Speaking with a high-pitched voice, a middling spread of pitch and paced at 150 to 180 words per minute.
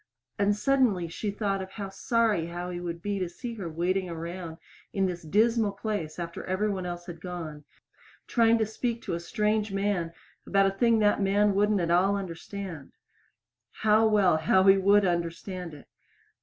Yes: high, 195 Hz; average, 3.3 semitones; average, 170 wpm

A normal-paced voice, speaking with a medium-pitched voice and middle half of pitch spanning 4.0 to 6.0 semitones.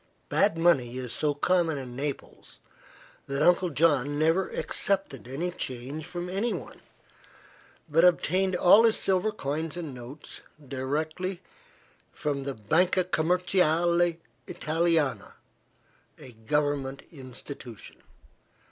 No: slow, 105 wpm; medium, 155 Hz; average, 4.4 semitones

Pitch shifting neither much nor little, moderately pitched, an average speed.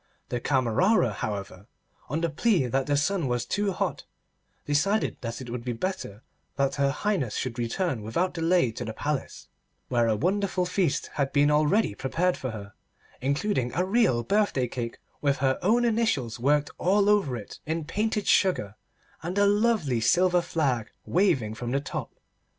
No: wide, 7.4 semitones; medium, 145 Hz; average, 165 wpm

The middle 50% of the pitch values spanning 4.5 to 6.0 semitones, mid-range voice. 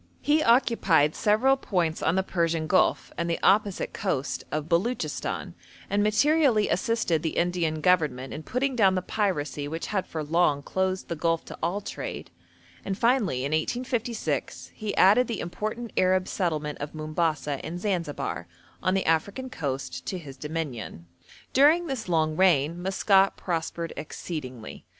Yes: average, 5.2 semitones; medium, 175 Hz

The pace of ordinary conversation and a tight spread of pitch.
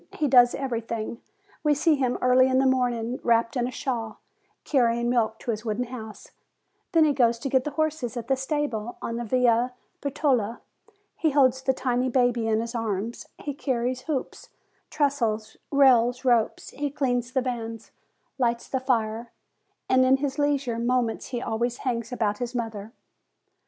Yes: average, 165 wpm; narrow, 2.3 semitones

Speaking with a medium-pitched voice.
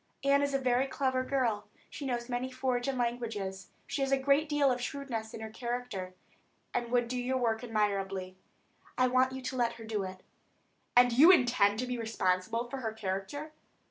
No: high, 245 Hz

